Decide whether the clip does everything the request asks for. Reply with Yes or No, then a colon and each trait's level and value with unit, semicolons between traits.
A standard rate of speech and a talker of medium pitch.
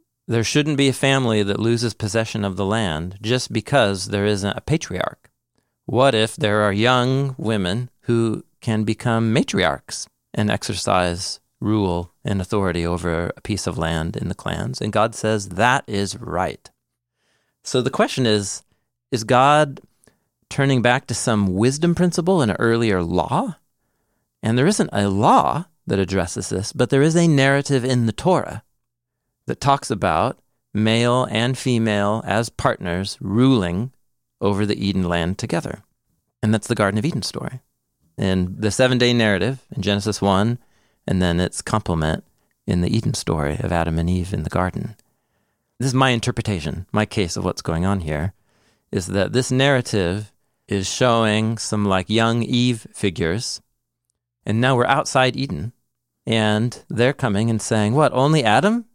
No: average, 160 wpm; low, 110 Hz